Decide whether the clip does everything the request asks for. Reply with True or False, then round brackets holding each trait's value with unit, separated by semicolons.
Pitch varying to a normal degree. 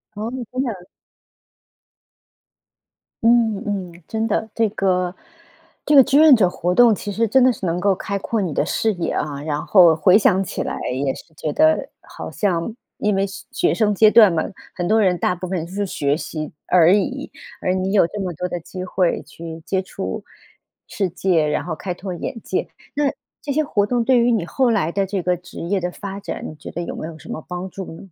True (3.9 semitones)